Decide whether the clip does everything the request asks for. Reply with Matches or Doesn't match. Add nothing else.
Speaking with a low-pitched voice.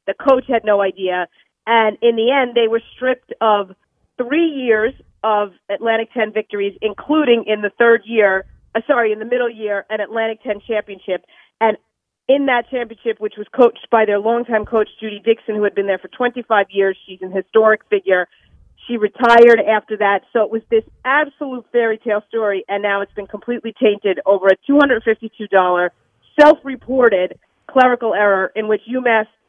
Doesn't match